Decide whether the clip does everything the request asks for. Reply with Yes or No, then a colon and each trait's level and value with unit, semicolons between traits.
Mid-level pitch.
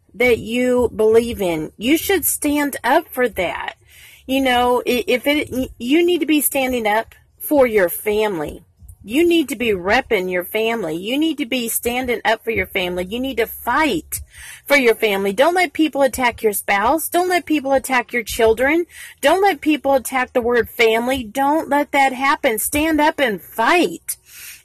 No: very high, 250 Hz